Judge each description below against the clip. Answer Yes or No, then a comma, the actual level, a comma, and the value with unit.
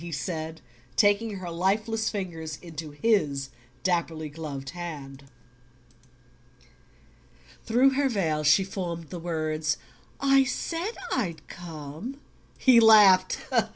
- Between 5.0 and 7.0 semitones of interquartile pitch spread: Yes, wide, 5.5 semitones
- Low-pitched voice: No, medium, 175 Hz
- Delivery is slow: Yes, slow, 105 wpm